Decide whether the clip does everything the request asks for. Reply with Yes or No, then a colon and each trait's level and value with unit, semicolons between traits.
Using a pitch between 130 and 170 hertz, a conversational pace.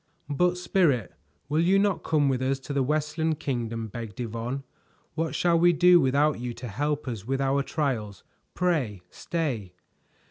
Yes: medium, 140 Hz; average, 165 wpm